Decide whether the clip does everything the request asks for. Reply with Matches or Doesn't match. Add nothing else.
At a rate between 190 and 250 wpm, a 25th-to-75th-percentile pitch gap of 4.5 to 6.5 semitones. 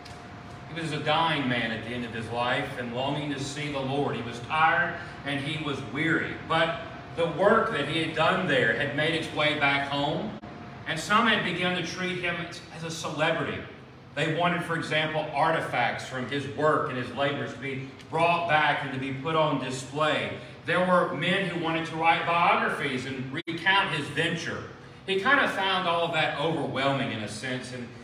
Doesn't match